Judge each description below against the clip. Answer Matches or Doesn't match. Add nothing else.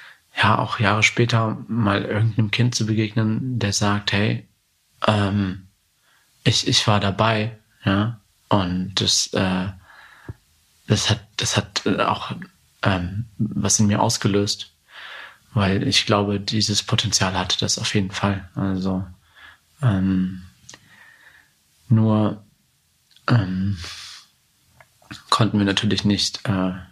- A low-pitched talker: Matches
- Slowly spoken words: Matches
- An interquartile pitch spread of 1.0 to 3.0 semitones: Matches